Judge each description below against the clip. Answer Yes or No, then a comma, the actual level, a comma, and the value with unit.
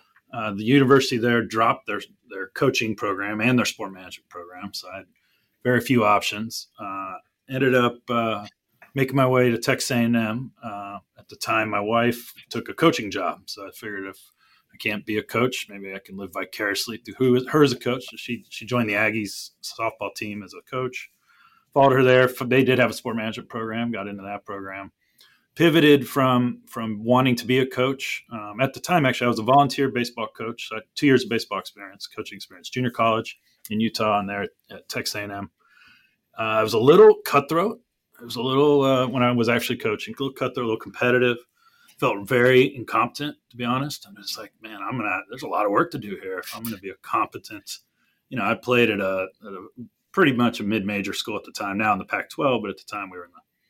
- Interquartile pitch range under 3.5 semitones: Yes, average, 2.9 semitones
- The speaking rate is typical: No, fast, 230 wpm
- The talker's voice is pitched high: No, low, 120 Hz